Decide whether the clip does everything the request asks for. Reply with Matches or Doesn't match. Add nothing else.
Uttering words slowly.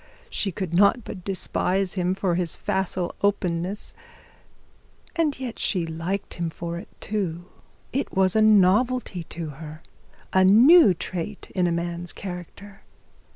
Matches